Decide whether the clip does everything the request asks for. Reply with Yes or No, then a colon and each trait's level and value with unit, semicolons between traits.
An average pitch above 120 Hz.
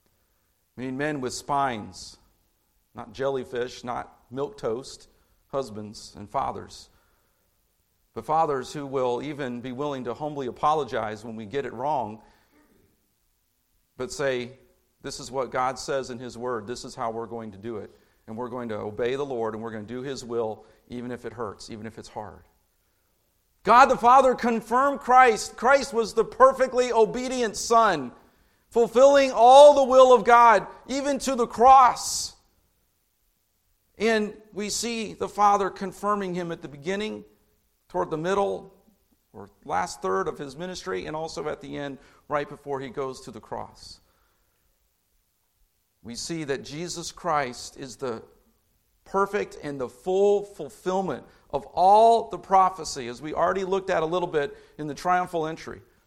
Yes: medium, 140 Hz